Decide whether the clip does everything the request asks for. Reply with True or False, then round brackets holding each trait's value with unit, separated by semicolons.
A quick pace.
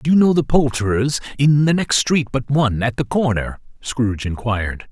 False (195 wpm)